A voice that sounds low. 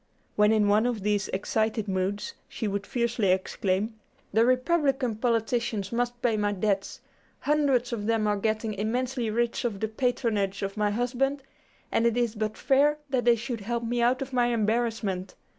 No: high, 225 Hz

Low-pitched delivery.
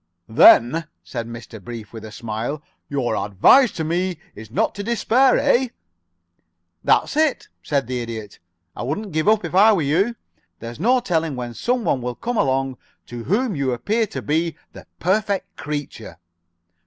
No: medium, 150 Hz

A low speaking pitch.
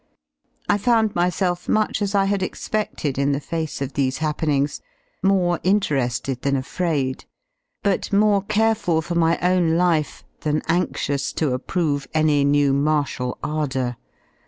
No: medium, 160 Hz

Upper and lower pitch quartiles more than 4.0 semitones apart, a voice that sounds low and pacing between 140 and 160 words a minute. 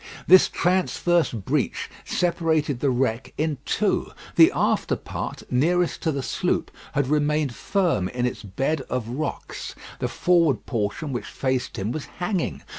No: average, 5.1 semitones; medium, 145 Hz; average, 145 wpm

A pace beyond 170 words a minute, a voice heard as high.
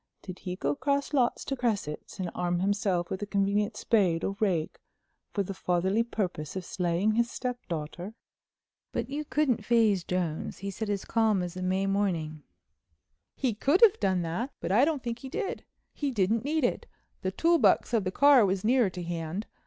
Yes: average, 190 wpm; high, 200 Hz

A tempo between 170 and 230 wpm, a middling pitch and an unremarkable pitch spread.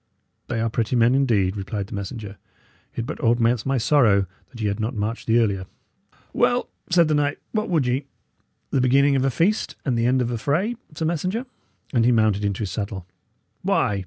No: average, 200 wpm; low, 120 Hz; average, 4.7 semitones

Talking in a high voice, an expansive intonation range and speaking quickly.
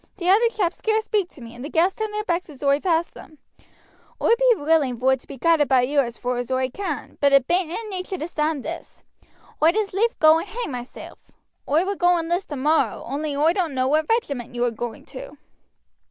Yes: very high, 320 Hz; wide, 5.8 semitones; fast, 230 wpm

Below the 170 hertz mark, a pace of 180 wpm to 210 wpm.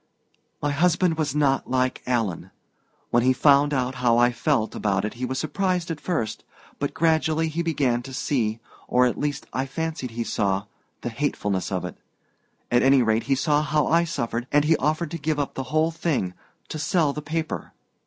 Yes: medium, 140 Hz; average, 195 wpm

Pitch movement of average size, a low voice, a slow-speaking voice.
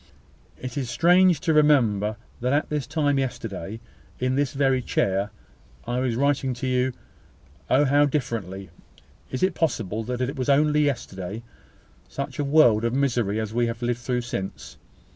No: average, 3.8 semitones; low, 130 Hz; average, 160 wpm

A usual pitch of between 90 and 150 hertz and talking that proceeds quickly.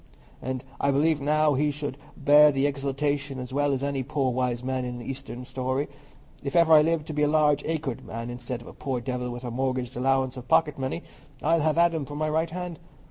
Yes: medium, 140 Hz; fast, 225 wpm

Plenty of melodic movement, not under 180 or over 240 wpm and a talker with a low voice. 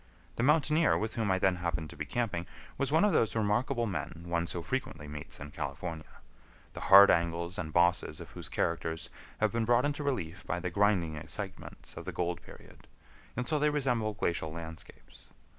Yes: wide, 6.0 semitones; average, 185 wpm; very low, 90 Hz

